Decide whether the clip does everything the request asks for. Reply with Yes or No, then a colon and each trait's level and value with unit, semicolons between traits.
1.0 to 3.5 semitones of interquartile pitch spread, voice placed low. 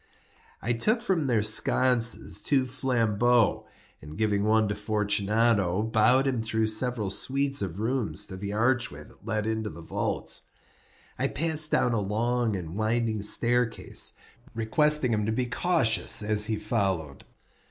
Yes: average, 2.9 semitones; low, 110 Hz